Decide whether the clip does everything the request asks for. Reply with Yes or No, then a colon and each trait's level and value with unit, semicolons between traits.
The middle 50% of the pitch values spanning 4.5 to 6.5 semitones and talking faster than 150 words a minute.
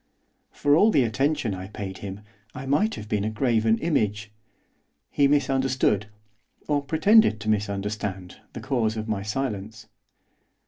No: average, 5.1 semitones; average, 140 wpm